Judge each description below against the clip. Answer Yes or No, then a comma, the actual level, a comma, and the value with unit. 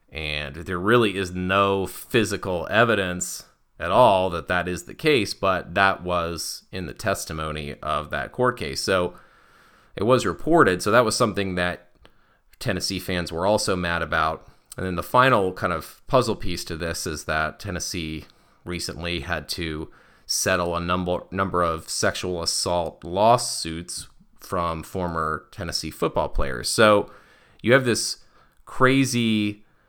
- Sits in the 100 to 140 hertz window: No, very low, 90 Hz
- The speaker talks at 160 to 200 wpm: No, average, 145 wpm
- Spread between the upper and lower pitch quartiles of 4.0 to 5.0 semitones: No, average, 2.9 semitones